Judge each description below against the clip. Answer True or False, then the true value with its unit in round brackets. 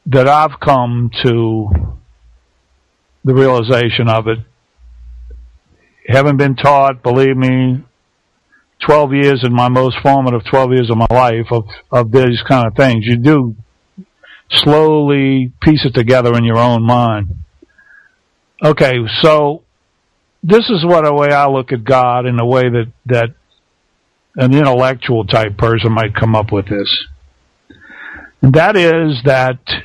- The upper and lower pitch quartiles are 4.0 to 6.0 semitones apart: False (3.6 semitones)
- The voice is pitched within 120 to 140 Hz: True (125 Hz)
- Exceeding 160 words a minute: False (140 wpm)